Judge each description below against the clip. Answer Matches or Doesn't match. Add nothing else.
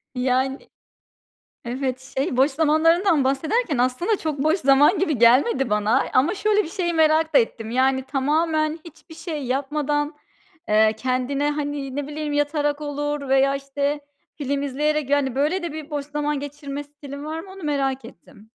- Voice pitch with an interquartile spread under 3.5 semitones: Matches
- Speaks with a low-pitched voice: Doesn't match